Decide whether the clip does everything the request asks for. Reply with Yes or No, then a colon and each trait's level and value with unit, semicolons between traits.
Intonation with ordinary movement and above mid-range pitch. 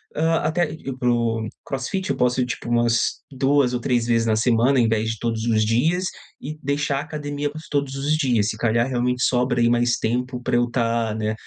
No: average, 3.3 semitones; low, 125 Hz